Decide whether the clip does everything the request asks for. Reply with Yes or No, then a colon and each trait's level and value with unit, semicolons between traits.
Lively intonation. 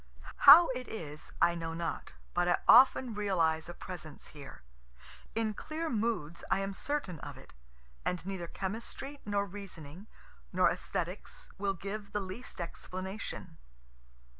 No: average, 4.6 semitones